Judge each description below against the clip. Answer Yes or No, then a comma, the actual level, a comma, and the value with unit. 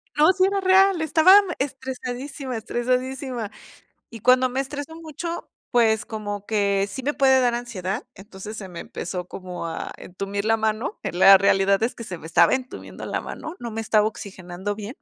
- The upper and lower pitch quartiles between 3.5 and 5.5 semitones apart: Yes, average, 5.1 semitones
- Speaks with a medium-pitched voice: No, high, 230 Hz